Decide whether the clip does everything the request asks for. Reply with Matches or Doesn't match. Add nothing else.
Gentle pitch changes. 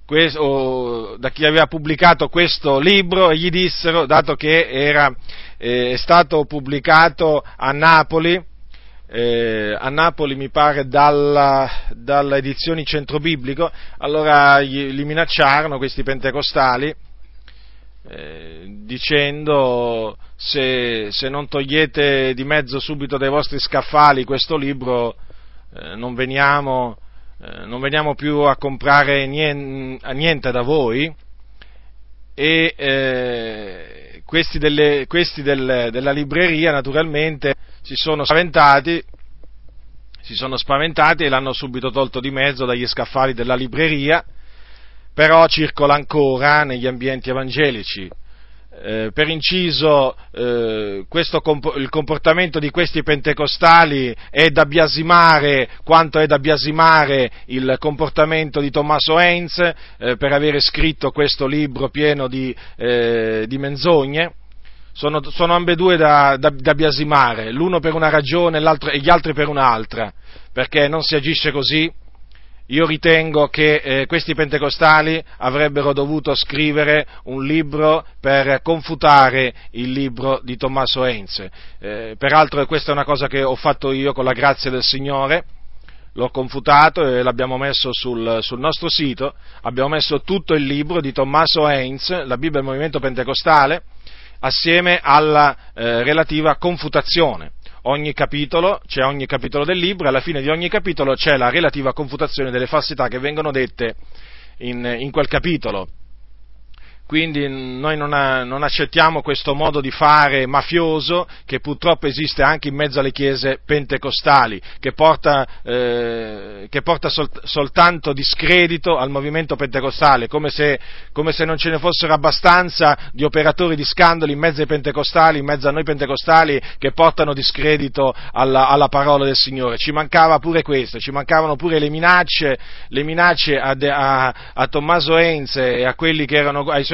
Doesn't match